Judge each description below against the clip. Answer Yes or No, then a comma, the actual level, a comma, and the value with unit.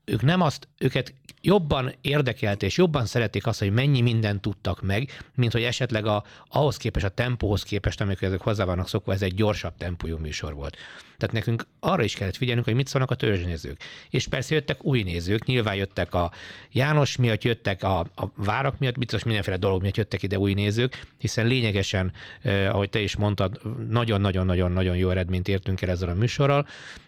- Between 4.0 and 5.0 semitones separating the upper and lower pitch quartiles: Yes, average, 4.3 semitones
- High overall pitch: No, low, 110 Hz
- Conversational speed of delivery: No, fast, 185 wpm